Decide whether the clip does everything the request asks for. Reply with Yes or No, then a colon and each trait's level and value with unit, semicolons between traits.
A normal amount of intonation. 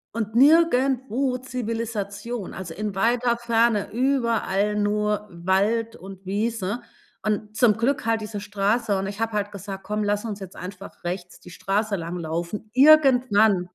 Yes: average, 3.1 semitones